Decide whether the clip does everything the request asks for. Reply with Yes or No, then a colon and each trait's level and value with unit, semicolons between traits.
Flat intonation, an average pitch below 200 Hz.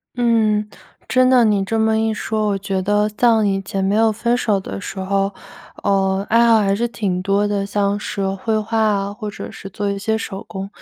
No: narrow, 2.1 semitones; high, 205 Hz